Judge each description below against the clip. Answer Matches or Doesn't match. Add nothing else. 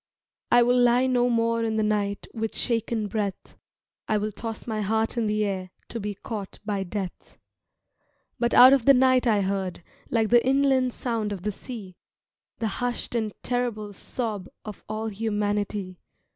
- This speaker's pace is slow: Doesn't match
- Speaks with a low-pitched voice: Doesn't match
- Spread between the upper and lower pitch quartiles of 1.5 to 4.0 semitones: Matches